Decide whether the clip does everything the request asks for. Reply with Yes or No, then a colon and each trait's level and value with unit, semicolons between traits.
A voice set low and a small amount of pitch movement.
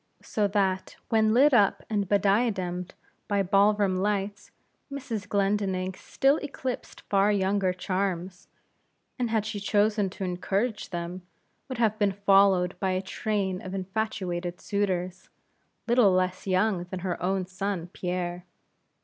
No: high, 195 Hz; narrow, 2.2 semitones